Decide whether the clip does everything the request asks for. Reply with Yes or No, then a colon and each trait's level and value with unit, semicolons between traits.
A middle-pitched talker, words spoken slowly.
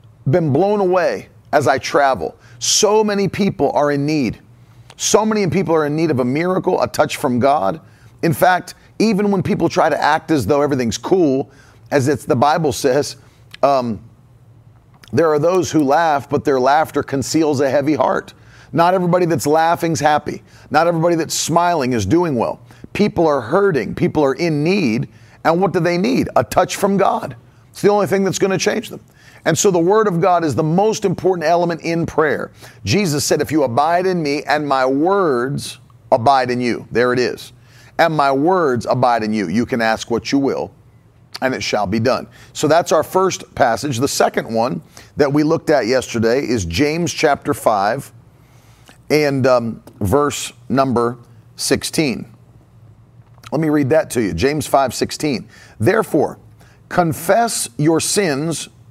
No: medium, 145 Hz; average, 175 wpm